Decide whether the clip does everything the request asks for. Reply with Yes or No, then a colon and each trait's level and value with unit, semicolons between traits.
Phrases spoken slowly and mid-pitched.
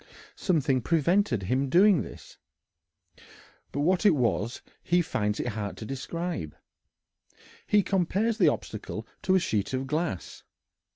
Yes: slow, 130 wpm; medium, 145 Hz